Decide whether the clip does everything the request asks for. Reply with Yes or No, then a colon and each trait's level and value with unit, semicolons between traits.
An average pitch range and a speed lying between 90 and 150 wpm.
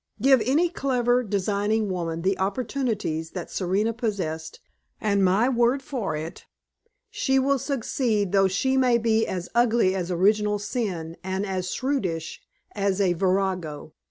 Yes: average, 4.5 semitones; slow, 135 wpm